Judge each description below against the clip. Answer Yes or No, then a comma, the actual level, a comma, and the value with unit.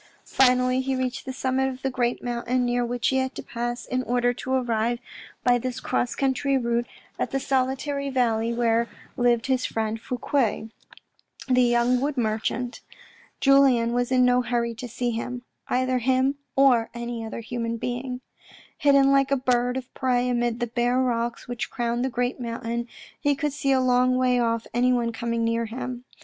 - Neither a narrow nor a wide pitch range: No, narrow, 1.5 semitones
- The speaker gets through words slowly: No, average, 180 wpm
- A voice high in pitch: Yes, high, 245 Hz